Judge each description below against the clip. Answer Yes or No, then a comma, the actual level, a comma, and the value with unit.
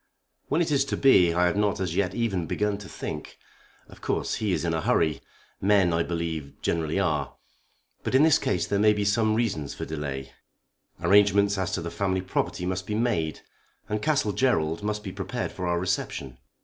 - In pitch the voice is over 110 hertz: No, very low, 95 Hz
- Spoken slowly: No, average, 200 wpm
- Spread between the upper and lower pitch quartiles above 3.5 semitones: Yes, average, 4.0 semitones